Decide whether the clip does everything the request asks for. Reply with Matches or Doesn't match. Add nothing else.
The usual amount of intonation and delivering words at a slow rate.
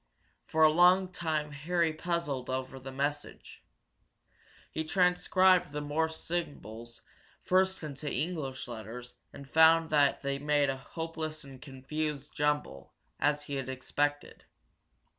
Matches